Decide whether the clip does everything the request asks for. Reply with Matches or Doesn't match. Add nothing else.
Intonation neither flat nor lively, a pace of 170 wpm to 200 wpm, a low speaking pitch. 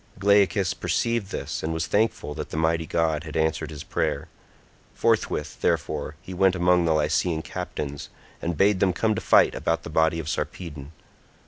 Matches